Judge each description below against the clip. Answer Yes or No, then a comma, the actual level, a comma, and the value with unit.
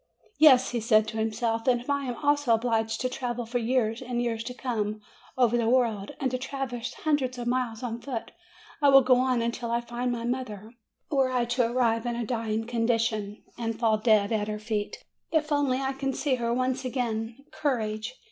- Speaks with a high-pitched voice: Yes, high, 240 Hz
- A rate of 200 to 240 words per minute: Yes, fast, 205 wpm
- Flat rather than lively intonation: Yes, narrow, 2.2 semitones